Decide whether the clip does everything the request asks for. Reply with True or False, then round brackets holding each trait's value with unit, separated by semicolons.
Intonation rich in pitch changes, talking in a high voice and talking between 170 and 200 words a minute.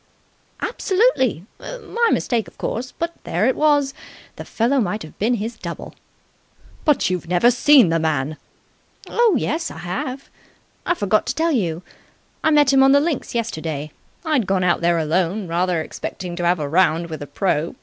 True (8.4 semitones; 205 Hz; 175 wpm)